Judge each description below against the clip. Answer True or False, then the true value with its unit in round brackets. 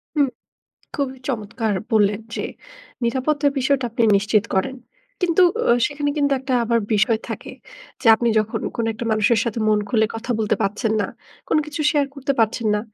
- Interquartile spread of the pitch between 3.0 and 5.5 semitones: True (4.4 semitones)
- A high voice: True (235 Hz)